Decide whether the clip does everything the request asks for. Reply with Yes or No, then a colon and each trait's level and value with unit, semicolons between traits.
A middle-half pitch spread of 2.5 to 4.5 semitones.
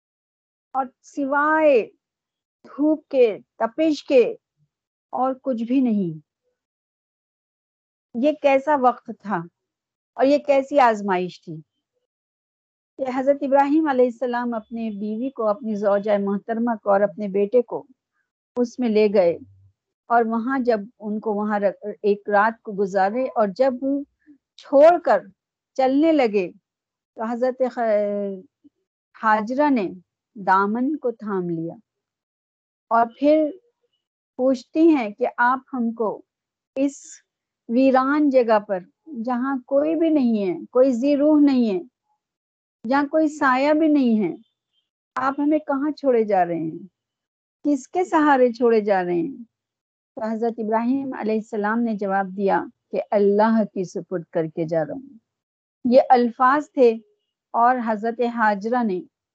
No: average, 5.2 semitones